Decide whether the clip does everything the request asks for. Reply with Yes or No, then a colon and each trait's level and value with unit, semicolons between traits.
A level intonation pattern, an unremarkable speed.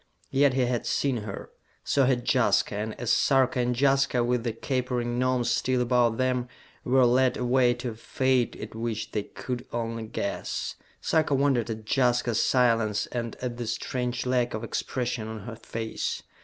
Yes: narrow, 1.8 semitones; average, 170 wpm